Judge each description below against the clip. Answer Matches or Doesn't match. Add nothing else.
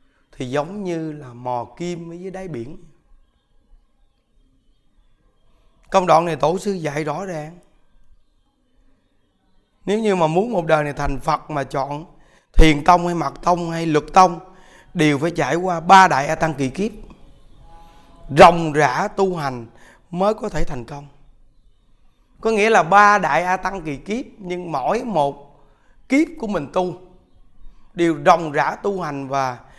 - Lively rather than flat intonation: Doesn't match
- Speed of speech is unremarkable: Doesn't match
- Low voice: Doesn't match